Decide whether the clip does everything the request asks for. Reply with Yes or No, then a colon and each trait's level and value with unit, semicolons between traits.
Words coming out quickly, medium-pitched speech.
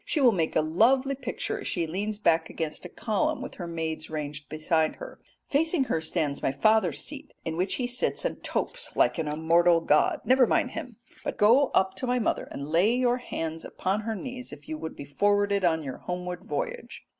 Yes: fast, 210 wpm; medium, 180 Hz